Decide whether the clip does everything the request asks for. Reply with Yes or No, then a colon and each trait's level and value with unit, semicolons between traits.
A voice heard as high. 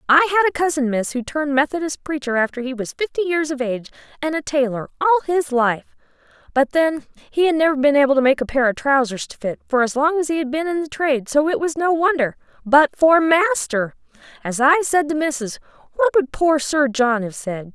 Yes: very high, 285 Hz